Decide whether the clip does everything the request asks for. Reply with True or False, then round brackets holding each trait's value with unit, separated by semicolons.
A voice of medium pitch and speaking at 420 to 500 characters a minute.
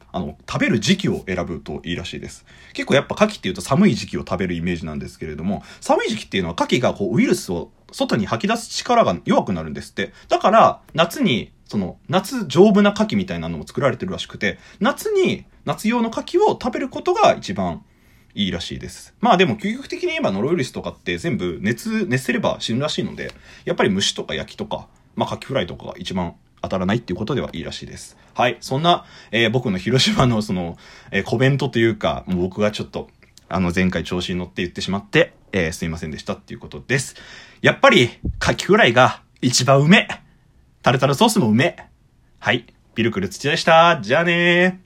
True (165 Hz; 435 characters per minute)